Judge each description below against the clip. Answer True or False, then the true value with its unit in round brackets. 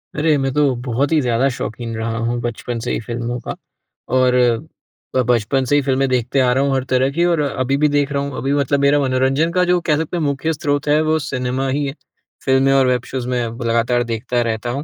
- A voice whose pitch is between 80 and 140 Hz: True (135 Hz)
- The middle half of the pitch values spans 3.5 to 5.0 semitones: False (2.8 semitones)